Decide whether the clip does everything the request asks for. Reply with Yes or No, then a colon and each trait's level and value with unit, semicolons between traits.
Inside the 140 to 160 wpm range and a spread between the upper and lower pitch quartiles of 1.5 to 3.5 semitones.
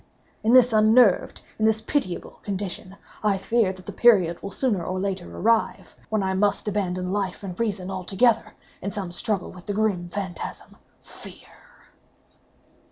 Yes: average, 145 wpm; average, 2.8 semitones